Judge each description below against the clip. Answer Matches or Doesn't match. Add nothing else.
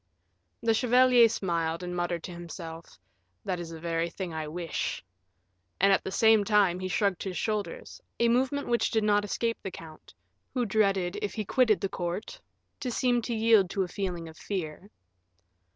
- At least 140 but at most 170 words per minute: Doesn't match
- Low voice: Doesn't match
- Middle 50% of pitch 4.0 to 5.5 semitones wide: Matches